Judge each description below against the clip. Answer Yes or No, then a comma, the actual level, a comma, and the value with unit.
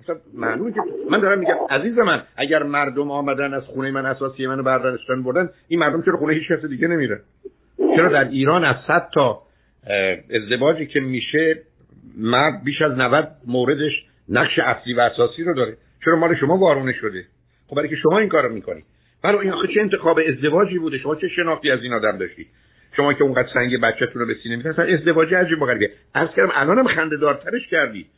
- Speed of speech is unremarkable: No, fast, 165 wpm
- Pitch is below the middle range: No, medium, 150 Hz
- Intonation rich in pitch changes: No, average, 4.4 semitones